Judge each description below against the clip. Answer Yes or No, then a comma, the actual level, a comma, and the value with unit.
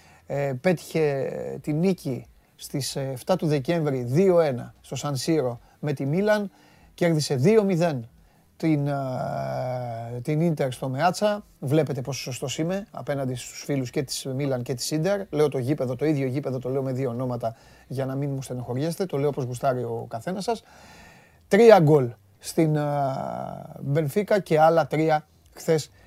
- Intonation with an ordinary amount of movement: Yes, average, 3.7 semitones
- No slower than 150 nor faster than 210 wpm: Yes, average, 155 wpm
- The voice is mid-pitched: Yes, medium, 145 Hz